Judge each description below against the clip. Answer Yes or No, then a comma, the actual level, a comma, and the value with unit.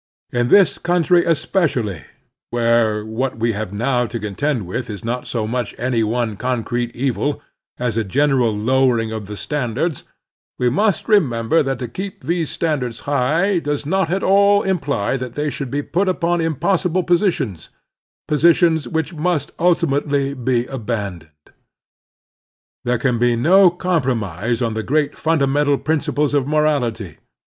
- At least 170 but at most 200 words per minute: No, average, 150 wpm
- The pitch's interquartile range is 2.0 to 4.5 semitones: No, wide, 5.6 semitones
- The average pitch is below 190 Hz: Yes, low, 135 Hz